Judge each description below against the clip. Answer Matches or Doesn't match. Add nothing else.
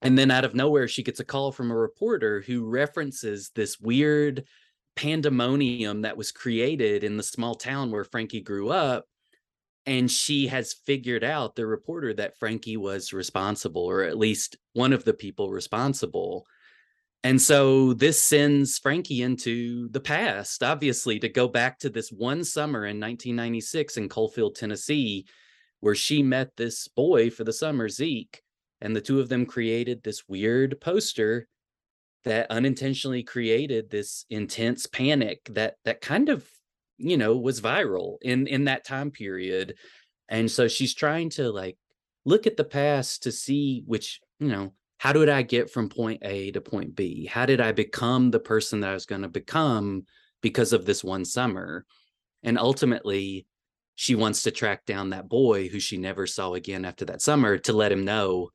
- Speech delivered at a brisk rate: Doesn't match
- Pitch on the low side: Matches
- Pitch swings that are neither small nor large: Matches